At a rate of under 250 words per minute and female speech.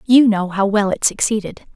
Yes: fast, 205 wpm; female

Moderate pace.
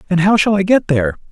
No: fast, 275 wpm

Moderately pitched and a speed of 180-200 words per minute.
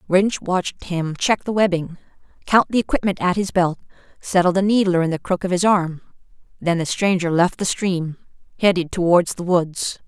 Yes: medium, 180 Hz; average, 185 wpm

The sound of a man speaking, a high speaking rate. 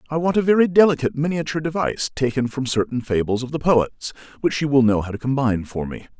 Yes: male; fast, 225 wpm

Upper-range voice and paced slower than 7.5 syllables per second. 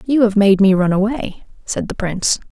Yes: high, 205 Hz; 5.2 syllables/s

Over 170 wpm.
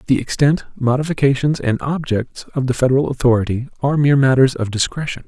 No: average, 160 wpm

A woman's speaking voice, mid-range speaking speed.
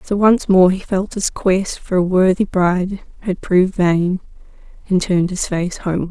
Yes: female; average, 185 wpm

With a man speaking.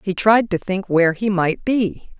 No: female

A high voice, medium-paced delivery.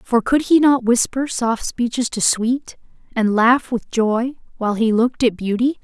Yes: high, 240 Hz; average, 185 wpm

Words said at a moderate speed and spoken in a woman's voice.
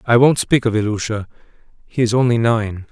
No: average, 185 wpm; male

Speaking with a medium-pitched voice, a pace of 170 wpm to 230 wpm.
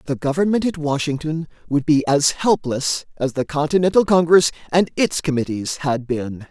No: medium, 150 Hz; average, 155 wpm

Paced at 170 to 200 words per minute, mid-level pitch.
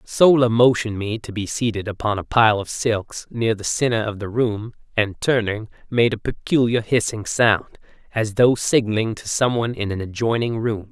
No: average, 180 wpm; low, 110 Hz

